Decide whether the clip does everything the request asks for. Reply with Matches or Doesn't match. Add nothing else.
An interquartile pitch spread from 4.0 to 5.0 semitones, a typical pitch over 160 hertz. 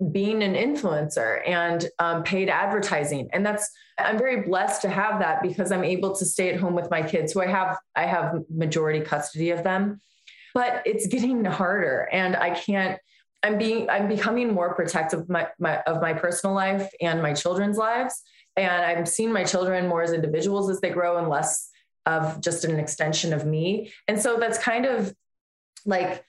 Doesn't match